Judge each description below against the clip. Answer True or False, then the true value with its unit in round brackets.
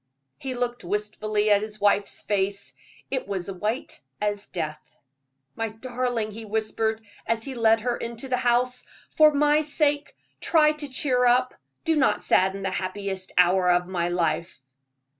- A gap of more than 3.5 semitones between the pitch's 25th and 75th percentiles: True (4.2 semitones)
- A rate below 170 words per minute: True (155 wpm)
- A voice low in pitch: False (220 Hz)